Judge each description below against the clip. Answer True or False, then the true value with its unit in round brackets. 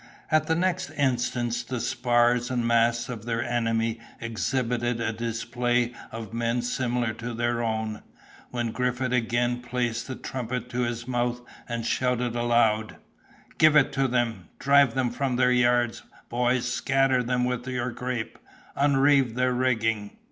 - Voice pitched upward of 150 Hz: False (120 Hz)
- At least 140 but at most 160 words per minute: True (145 wpm)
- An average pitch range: False (1.2 semitones)